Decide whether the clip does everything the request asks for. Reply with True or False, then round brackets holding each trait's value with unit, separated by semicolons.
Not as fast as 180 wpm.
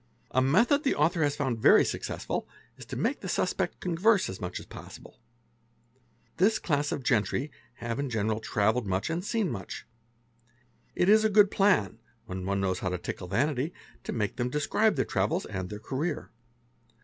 False (185 wpm)